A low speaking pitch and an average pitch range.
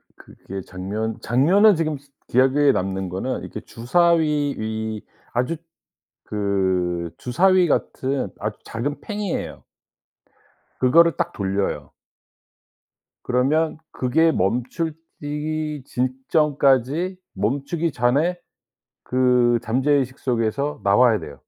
No: low, 130 Hz; wide, 5.8 semitones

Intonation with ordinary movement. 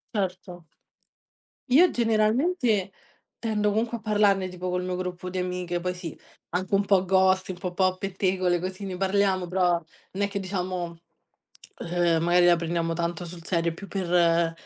No: narrow, 2.0 semitones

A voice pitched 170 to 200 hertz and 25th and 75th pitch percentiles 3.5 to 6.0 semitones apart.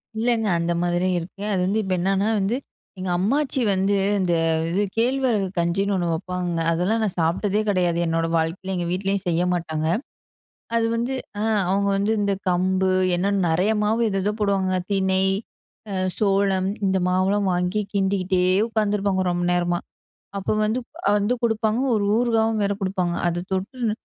No: high, 195 Hz; narrow, 2.6 semitones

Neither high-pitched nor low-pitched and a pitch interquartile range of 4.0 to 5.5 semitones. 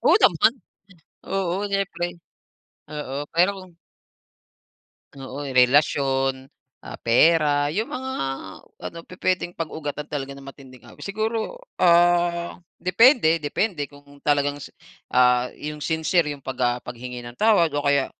Yes: medium, 150 Hz; average, 4.5 semitones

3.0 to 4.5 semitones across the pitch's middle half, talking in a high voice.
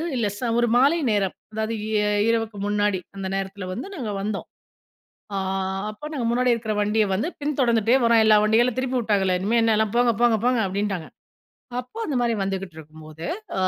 Yes: average, 3.4 semitones; high, 220 Hz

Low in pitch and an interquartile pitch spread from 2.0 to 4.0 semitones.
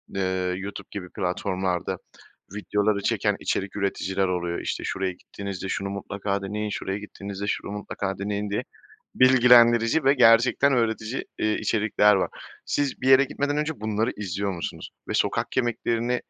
Yes: low, 105 Hz; average, 3.2 semitones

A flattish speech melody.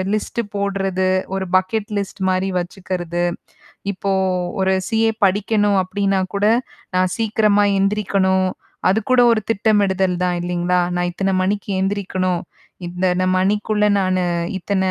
Yes: narrow, 1.8 semitones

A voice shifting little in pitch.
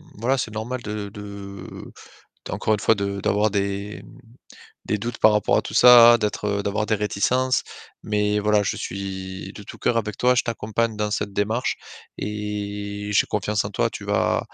Yes: narrow, 1.4 semitones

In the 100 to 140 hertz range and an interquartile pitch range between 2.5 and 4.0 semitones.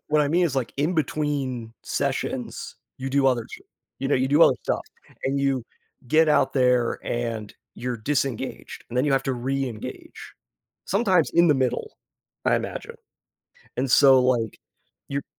Yes: low, 135 Hz; average, 2.8 semitones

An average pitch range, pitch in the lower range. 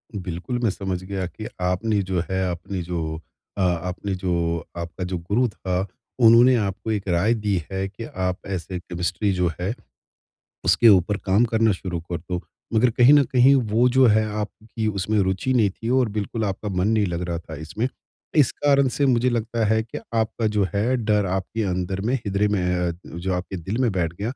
Yes: average, 3.7 semitones; low, 100 Hz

